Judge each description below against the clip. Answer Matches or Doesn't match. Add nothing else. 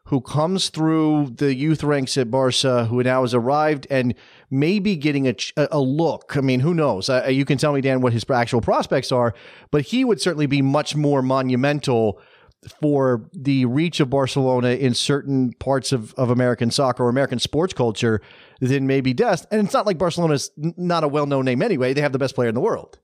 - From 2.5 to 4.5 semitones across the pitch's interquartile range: Matches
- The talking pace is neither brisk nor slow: Doesn't match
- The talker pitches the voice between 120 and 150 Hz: Matches